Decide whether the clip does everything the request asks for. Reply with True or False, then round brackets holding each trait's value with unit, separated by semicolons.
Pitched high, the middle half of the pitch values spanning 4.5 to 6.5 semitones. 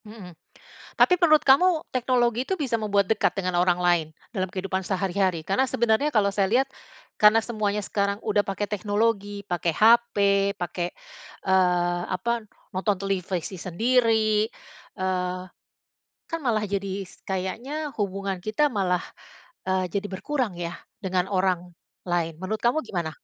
False (200 Hz; 3.4 semitones)